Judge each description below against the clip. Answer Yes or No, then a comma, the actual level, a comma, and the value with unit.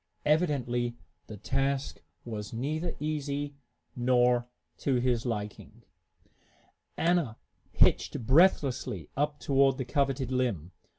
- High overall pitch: No, low, 130 Hz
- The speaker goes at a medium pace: No, slow, 100 wpm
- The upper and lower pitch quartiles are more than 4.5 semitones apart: No, average, 3.3 semitones